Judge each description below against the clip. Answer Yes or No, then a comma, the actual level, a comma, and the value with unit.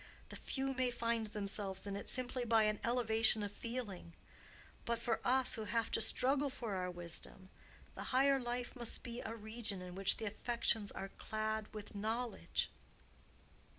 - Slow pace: No, average, 165 wpm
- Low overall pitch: No, high, 225 Hz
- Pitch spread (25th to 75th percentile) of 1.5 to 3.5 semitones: Yes, average, 2.9 semitones